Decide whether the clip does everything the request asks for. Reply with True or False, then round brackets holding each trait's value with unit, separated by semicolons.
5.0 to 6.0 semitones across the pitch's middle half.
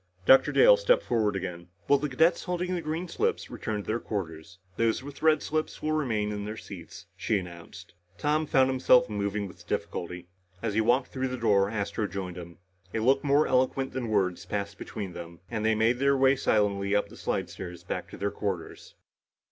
True (5.3 semitones)